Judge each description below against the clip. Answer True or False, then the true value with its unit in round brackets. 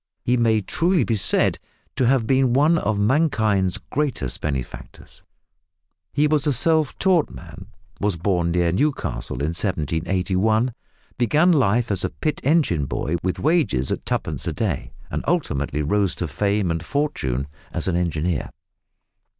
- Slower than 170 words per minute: True (150 wpm)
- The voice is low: True (105 Hz)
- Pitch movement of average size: False (8.7 semitones)